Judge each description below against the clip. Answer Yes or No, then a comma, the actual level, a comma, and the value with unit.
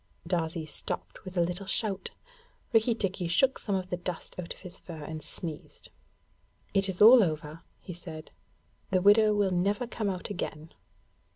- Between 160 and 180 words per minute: Yes, average, 170 wpm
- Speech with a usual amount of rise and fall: Yes, average, 3.3 semitones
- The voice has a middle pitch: Yes, medium, 180 Hz